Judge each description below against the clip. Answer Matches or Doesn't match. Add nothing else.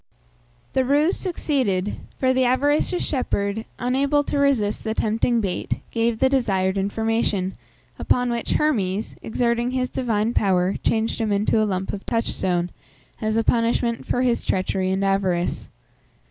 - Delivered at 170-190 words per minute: Doesn't match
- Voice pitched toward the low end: Doesn't match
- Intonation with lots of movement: Doesn't match